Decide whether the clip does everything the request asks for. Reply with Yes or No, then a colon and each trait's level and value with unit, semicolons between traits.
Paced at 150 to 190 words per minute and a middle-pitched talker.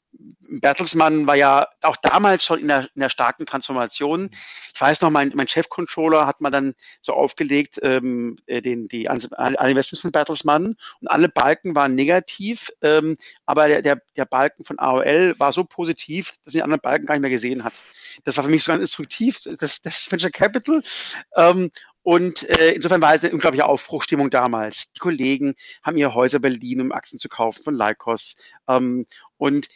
Yes: average, 185 wpm; medium, 145 Hz